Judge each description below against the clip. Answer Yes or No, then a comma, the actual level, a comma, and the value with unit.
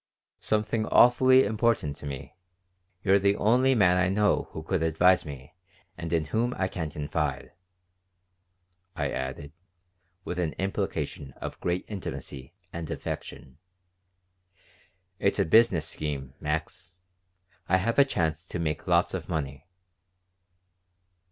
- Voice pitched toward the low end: Yes, very low, 85 Hz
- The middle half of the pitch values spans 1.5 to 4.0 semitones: No, average, 4.8 semitones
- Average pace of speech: No, slow, 125 wpm